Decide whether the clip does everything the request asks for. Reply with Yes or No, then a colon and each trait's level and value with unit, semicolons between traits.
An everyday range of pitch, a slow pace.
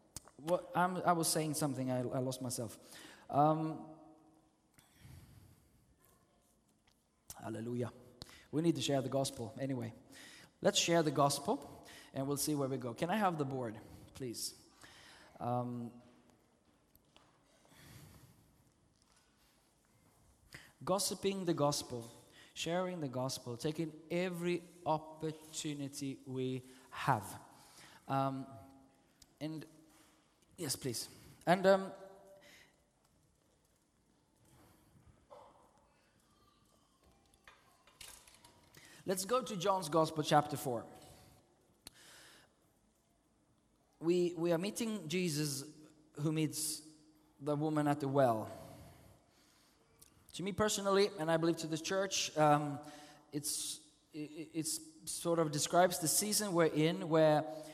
Yes: average, 3.7 semitones; slow, 95 wpm